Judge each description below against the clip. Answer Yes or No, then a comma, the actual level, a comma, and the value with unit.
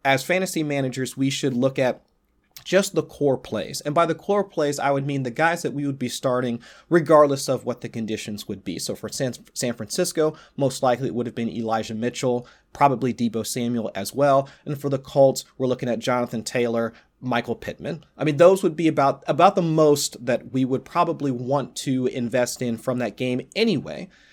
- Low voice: Yes, low, 130 Hz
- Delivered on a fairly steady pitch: No, average, 3.7 semitones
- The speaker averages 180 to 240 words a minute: Yes, average, 200 wpm